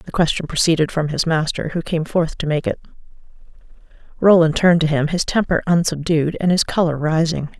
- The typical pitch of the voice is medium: Yes, medium, 160 Hz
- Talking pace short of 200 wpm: Yes, average, 180 wpm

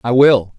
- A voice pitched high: No, low, 120 Hz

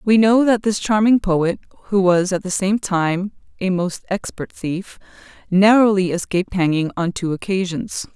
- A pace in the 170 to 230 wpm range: No, average, 160 wpm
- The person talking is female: Yes, female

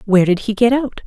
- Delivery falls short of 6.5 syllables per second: No, 6.7 syllables/s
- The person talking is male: No, female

